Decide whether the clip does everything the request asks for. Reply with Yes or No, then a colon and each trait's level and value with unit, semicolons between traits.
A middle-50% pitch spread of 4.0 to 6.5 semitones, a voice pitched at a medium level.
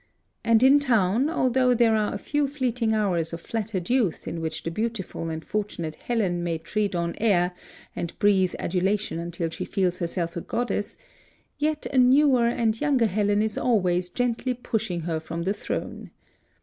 No: wide, 5.6 semitones; high, 210 Hz